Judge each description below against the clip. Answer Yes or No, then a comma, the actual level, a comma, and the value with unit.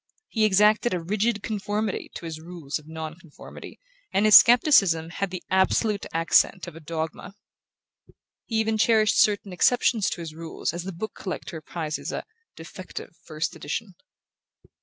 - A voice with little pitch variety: No, average, 4.6 semitones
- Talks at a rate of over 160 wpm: No, average, 155 wpm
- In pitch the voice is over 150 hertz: Yes, medium, 185 Hz